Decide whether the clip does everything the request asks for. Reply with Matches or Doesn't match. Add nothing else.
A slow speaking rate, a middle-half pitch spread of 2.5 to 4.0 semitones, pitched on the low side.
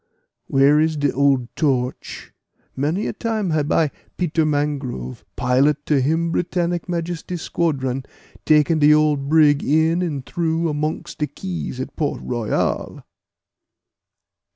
Doesn't match